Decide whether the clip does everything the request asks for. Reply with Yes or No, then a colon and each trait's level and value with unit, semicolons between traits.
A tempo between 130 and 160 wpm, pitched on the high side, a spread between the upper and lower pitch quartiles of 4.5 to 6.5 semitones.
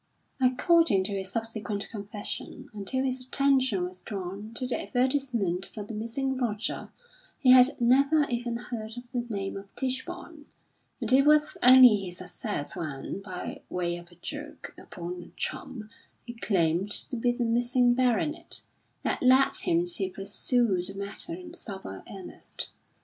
Yes: average, 155 wpm; high, 235 Hz; average, 4.9 semitones